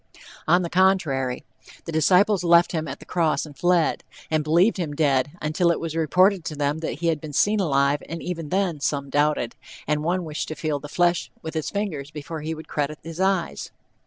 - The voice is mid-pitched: Yes, medium, 160 Hz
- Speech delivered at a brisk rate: Yes, fast, 210 wpm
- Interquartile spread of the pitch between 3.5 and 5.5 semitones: No, average, 3.0 semitones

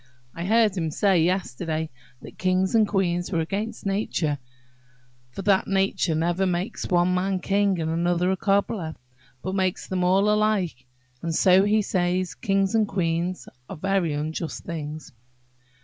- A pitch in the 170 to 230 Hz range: Yes, medium, 185 Hz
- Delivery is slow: No, average, 155 wpm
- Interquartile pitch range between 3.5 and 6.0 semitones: No, average, 2.7 semitones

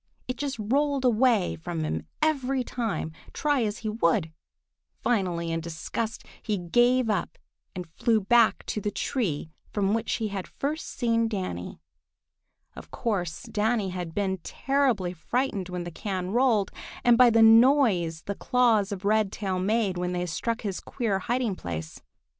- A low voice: No, high, 210 Hz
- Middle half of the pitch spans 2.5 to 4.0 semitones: No, average, 4.9 semitones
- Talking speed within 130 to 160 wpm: Yes, average, 155 wpm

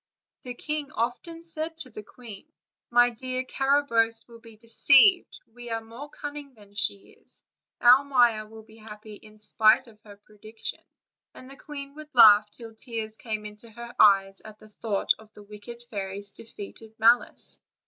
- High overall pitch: Yes, high, 225 Hz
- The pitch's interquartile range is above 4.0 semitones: No, average, 3.2 semitones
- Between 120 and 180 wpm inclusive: Yes, average, 170 wpm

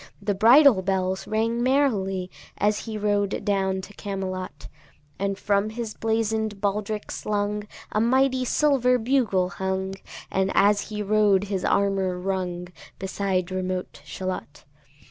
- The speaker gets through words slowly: Yes, slow, 125 wpm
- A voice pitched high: Yes, high, 200 Hz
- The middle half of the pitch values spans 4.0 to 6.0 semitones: No, narrow, 2.5 semitones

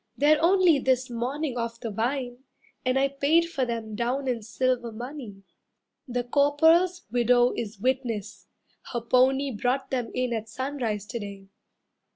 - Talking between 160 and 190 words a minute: No, average, 150 wpm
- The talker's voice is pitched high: Yes, very high, 250 Hz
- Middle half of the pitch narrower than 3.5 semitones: Yes, average, 3.0 semitones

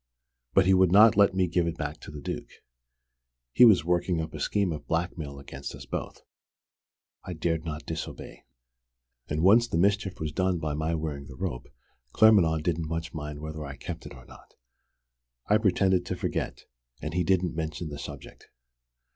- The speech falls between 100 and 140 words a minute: No, average, 180 wpm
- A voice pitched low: Yes, very low, 80 Hz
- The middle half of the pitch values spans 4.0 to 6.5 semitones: No, average, 3.4 semitones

